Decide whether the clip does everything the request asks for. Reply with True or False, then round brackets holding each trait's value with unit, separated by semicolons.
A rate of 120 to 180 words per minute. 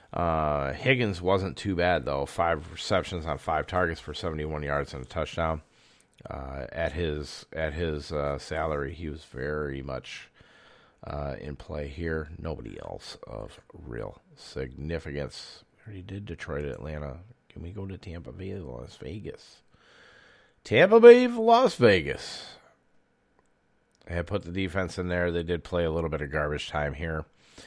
True (155 wpm)